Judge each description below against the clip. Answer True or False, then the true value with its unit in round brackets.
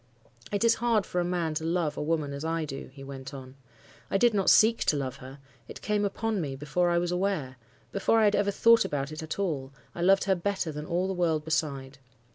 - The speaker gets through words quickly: True (230 wpm)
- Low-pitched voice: False (165 Hz)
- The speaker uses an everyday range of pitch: False (5.7 semitones)